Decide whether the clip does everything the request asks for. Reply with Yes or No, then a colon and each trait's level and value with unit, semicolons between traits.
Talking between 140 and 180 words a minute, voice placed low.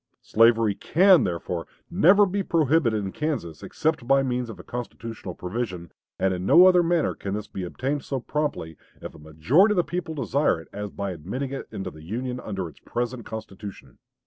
No: average, 190 wpm; low, 120 Hz